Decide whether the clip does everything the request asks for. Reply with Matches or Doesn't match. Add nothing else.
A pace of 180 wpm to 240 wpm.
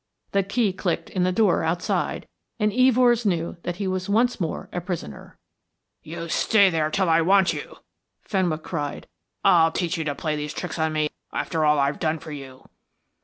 Matches